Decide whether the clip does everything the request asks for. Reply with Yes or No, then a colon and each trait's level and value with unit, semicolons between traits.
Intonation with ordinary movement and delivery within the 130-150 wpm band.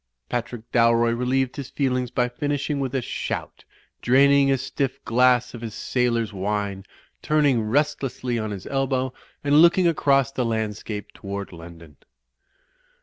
Yes: average, 3.6 semitones; average, 140 wpm